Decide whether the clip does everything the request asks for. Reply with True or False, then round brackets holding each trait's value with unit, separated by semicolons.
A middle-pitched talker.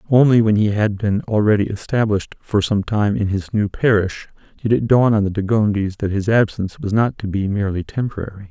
False (105 Hz)